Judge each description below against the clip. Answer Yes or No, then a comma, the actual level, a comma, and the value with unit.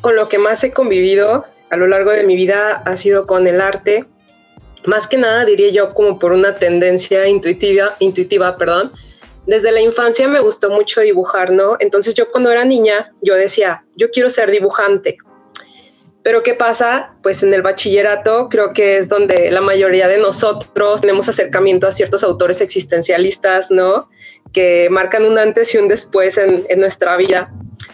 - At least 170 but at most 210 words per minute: Yes, average, 175 wpm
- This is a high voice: Yes, high, 200 Hz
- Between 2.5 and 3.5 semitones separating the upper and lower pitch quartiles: Yes, average, 2.9 semitones